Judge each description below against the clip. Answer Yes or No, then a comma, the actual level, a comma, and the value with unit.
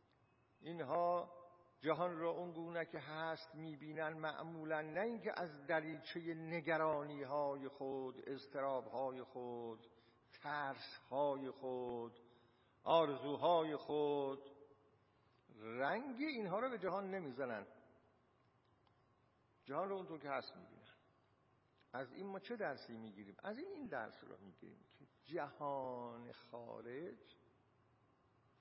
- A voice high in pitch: No, medium, 140 Hz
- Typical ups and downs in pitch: Yes, average, 4.8 semitones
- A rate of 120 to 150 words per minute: No, slow, 105 wpm